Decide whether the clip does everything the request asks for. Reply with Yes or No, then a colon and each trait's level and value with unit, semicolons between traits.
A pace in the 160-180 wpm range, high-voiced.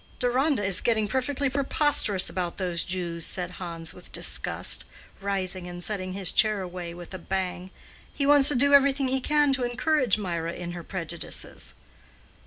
Yes: average, 165 wpm; high, 195 Hz